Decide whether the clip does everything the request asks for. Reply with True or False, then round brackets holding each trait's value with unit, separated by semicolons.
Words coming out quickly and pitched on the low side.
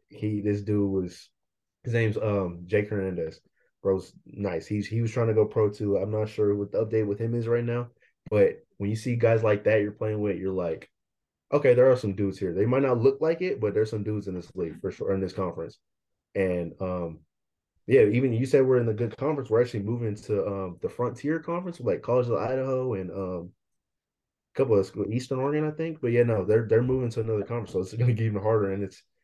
True (240 wpm; 110 Hz)